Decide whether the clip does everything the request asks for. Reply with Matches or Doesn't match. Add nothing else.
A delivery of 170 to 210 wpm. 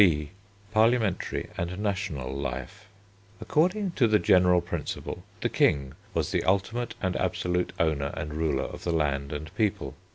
Doesn't match